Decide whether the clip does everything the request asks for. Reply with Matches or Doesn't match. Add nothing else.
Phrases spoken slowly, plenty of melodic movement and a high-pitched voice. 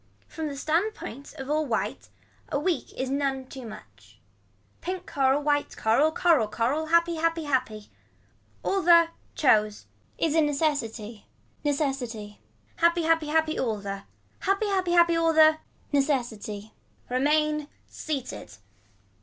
Doesn't match